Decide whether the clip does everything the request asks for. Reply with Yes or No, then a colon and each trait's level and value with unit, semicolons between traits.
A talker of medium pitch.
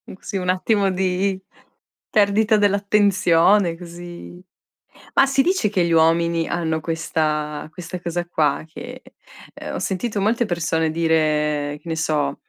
Yes: medium, 175 Hz